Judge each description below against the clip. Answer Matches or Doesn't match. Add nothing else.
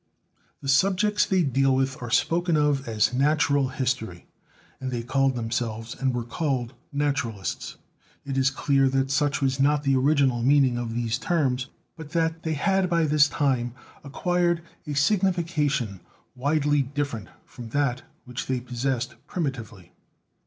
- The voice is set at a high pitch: Doesn't match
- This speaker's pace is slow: Doesn't match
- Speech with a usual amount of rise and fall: Matches